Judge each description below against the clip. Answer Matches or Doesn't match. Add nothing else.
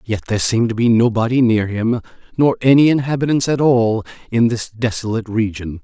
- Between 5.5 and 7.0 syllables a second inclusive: Matches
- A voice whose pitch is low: Matches